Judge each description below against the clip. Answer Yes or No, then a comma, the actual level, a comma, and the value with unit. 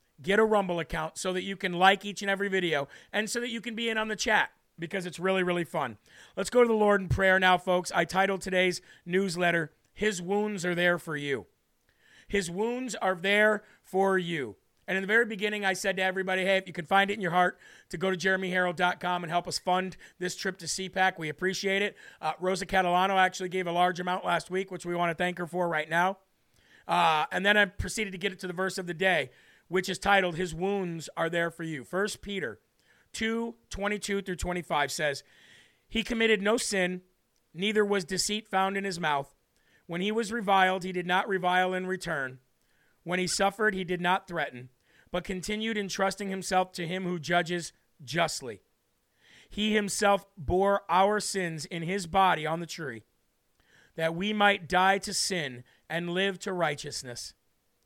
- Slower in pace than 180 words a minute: No, average, 200 wpm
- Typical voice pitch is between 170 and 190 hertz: Yes, medium, 185 Hz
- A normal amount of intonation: No, narrow, 2.2 semitones